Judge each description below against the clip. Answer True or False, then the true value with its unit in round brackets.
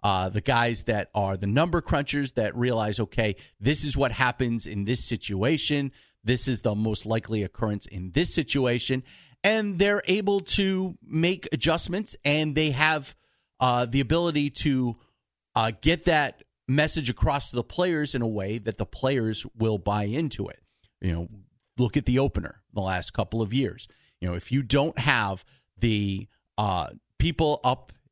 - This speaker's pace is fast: False (170 wpm)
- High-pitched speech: False (125 Hz)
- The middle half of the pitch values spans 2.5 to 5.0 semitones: False (5.6 semitones)